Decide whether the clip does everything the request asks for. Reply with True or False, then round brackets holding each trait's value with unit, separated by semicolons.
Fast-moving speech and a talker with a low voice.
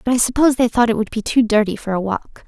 False (315 wpm; 230 Hz)